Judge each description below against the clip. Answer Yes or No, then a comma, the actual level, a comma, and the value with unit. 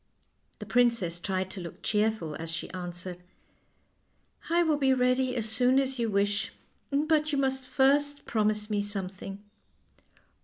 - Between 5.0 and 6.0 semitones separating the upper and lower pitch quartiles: Yes, wide, 5.6 semitones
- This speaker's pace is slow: No, average, 150 wpm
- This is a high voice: Yes, high, 220 Hz